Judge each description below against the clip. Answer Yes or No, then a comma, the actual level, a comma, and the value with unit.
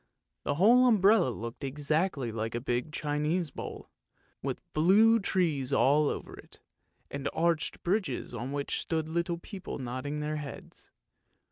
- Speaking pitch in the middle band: Yes, medium, 150 Hz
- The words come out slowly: No, average, 145 wpm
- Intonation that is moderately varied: Yes, average, 4.7 semitones